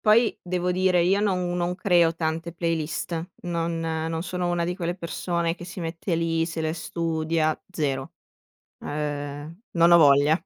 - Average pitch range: No, narrow, 1.7 semitones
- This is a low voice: No, medium, 170 Hz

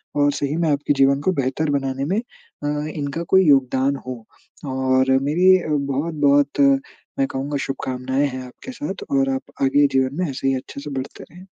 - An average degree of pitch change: No, narrow, 2.0 semitones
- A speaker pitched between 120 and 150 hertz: Yes, medium, 140 Hz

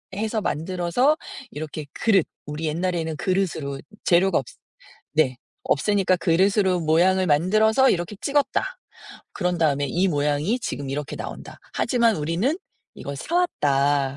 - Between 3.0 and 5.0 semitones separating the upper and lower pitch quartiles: No, wide, 5.5 semitones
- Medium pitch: Yes, medium, 175 Hz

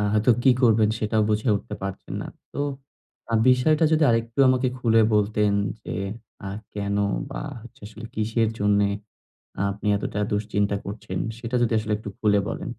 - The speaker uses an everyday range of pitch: No, narrow, 2.3 semitones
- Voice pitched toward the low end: Yes, low, 110 Hz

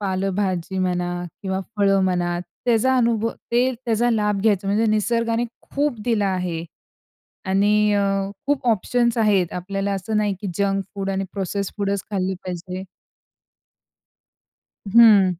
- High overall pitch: Yes, high, 200 Hz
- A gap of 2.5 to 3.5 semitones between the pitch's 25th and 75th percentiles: Yes, average, 2.9 semitones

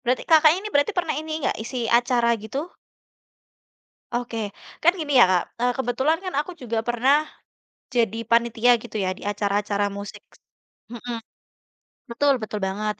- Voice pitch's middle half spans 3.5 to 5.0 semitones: Yes, average, 4.4 semitones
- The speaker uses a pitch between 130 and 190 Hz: No, high, 240 Hz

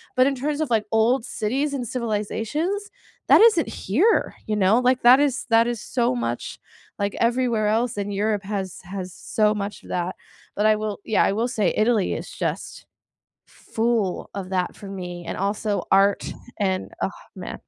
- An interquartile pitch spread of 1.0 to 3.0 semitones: No, average, 3.7 semitones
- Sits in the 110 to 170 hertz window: No, high, 215 Hz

